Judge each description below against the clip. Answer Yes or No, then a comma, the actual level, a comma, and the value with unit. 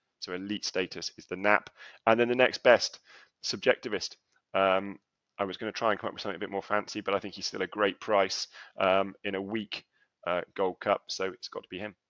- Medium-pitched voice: No, low, 100 Hz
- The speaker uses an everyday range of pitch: No, narrow, 2.1 semitones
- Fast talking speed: Yes, fast, 240 wpm